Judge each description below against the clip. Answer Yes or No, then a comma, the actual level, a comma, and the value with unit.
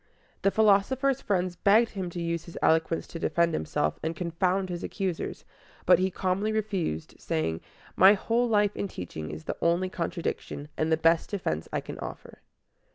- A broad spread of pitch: No, average, 3.5 semitones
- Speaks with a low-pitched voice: No, medium, 180 Hz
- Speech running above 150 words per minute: Yes, average, 170 wpm